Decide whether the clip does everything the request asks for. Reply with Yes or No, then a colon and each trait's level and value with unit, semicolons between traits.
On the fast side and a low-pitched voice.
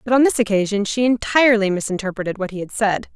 No: fast, 210 wpm; high, 215 Hz